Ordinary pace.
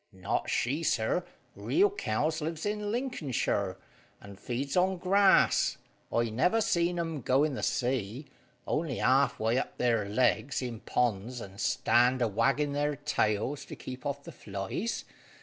Yes: average, 150 wpm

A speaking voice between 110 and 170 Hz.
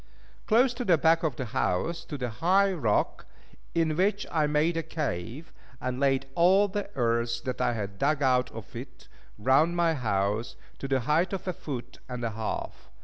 Yes: medium, 140 Hz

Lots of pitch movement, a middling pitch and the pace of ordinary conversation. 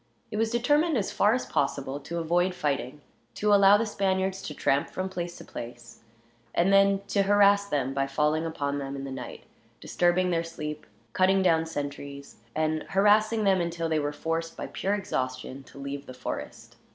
Yes: wide, 5.7 semitones; medium, 165 Hz; average, 185 wpm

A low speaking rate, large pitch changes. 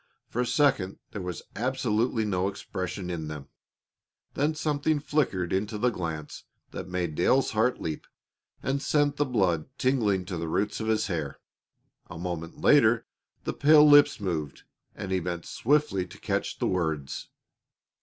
No: average, 155 wpm; wide, 7.1 semitones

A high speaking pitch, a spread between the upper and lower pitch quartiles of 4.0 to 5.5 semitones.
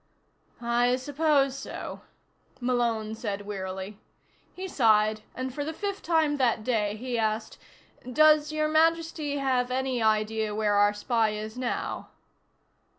Yes: high, 245 Hz; average, 5.1 semitones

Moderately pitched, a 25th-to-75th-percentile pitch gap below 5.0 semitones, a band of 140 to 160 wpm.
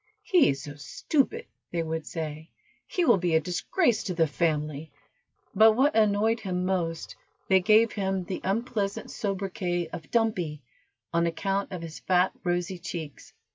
Yes: medium, 180 Hz; average, 4.4 semitones; average, 155 wpm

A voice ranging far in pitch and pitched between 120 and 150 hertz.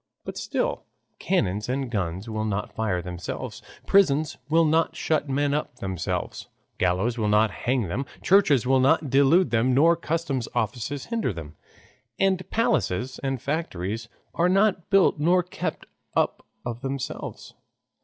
Yes: wide, 7.1 semitones; low, 135 Hz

